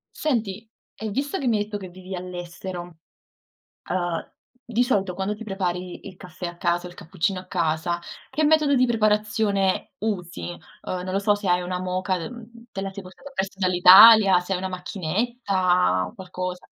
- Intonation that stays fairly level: No, average, 3.1 semitones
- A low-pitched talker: No, high, 190 Hz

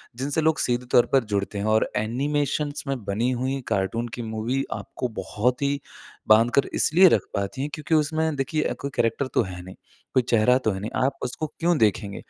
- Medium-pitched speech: No, low, 125 Hz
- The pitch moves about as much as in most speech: Yes, average, 4.7 semitones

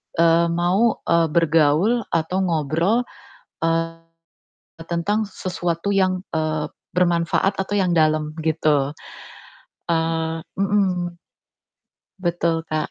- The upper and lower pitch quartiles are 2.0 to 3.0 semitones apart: Yes, narrow, 2.4 semitones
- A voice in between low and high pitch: Yes, medium, 170 Hz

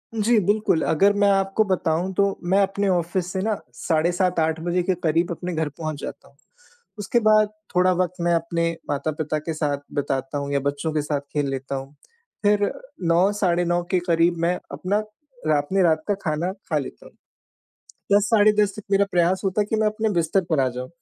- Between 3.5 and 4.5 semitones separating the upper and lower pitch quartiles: Yes, average, 4.0 semitones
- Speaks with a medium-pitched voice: Yes, medium, 175 Hz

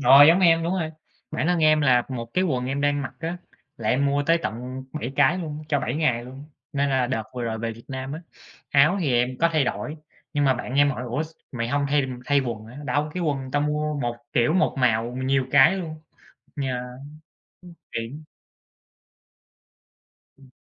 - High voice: No, medium, 140 Hz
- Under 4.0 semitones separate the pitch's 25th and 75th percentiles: Yes, average, 3.4 semitones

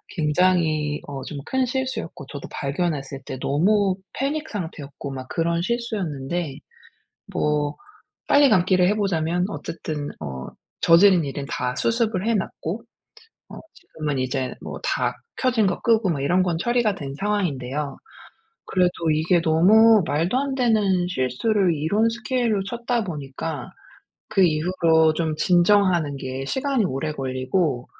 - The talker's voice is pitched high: No, medium, 170 Hz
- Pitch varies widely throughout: Yes, wide, 6.2 semitones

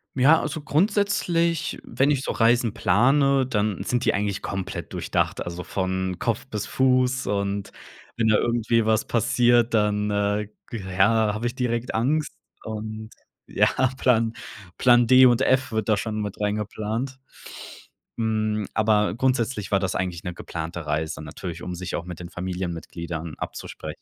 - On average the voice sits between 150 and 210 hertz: No, low, 110 Hz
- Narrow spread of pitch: No, average, 4.3 semitones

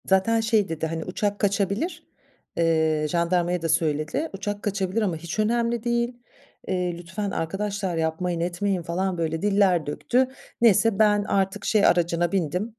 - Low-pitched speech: No, high, 190 Hz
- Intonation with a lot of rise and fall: No, average, 3.6 semitones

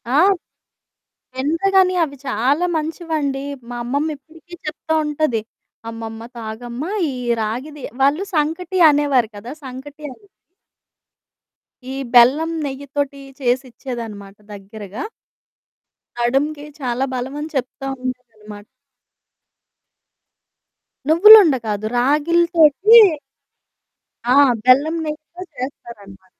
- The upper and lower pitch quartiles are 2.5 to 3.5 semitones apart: No, average, 4.4 semitones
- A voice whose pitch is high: Yes, very high, 270 Hz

